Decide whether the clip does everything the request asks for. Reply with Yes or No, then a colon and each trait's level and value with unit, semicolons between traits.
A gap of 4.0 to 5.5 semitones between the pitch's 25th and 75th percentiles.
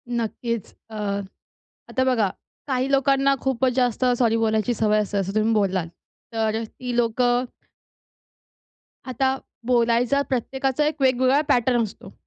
No: average, 2.9 semitones